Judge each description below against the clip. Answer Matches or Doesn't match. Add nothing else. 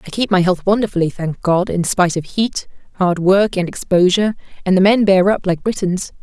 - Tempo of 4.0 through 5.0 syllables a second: Doesn't match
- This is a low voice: Doesn't match